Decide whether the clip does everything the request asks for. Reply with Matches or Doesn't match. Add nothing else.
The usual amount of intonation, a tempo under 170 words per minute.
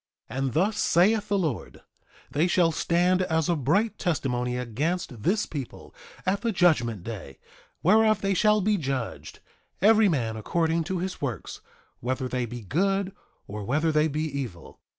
Doesn't match